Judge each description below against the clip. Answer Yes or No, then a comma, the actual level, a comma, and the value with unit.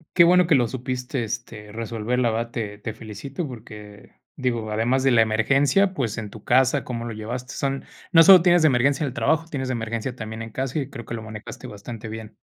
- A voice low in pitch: Yes, low, 120 Hz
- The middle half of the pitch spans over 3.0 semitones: Yes, average, 3.6 semitones